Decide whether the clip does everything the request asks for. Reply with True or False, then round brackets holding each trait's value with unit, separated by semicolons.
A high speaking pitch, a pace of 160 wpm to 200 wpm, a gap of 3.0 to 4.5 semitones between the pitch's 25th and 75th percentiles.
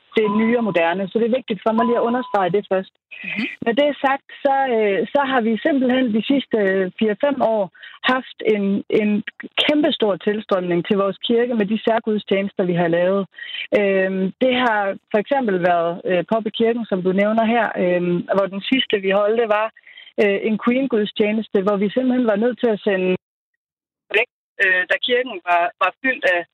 True (215 Hz; 175 wpm; 4.0 semitones)